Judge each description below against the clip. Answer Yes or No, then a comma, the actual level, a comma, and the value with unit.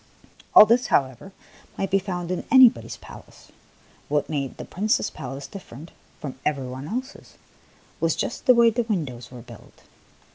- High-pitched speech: No, medium, 175 Hz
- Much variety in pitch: Yes, wide, 8.2 semitones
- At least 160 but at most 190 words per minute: Yes, average, 170 wpm